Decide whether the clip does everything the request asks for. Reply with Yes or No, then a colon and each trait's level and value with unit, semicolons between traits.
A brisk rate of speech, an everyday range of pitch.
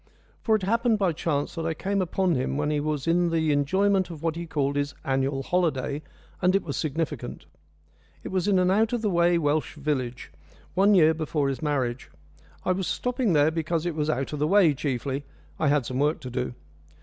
Yes: fast, 210 wpm; average, 4.2 semitones